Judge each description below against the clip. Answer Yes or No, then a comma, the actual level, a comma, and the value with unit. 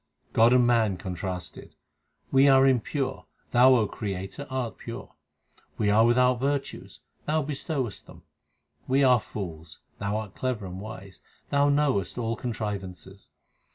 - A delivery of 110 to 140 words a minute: Yes, slow, 135 wpm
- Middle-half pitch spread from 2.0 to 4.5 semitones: No, average, 5.1 semitones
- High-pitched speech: No, low, 115 Hz